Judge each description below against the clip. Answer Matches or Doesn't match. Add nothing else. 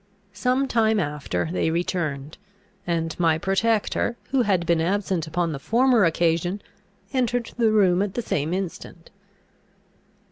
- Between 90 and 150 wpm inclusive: Matches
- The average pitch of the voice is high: Doesn't match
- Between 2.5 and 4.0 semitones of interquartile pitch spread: Doesn't match